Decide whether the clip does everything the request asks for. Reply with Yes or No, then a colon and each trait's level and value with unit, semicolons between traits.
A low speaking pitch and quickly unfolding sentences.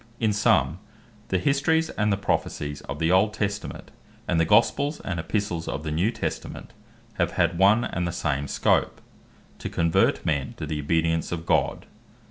No: very low, 85 Hz; average, 175 wpm